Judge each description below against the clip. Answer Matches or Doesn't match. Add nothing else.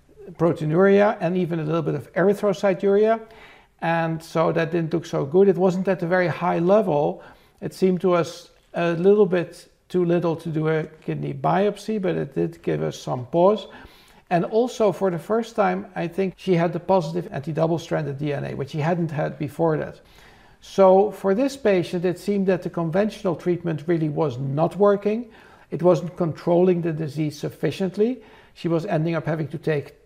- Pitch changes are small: Doesn't match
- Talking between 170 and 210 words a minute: Matches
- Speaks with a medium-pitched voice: Matches